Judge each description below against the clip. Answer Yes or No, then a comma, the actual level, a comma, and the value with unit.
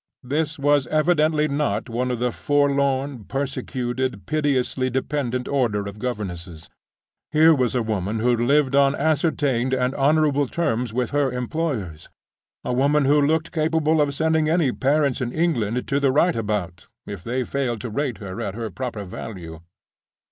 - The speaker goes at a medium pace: Yes, average, 155 wpm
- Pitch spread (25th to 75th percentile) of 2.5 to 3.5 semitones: No, average, 4.0 semitones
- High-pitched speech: No, low, 130 Hz